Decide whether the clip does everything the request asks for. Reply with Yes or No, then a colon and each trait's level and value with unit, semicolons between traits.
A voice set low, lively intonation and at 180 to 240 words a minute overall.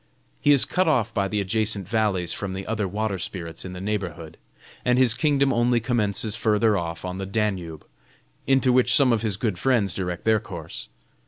No: low, 105 Hz; average, 4.0 semitones; average, 190 wpm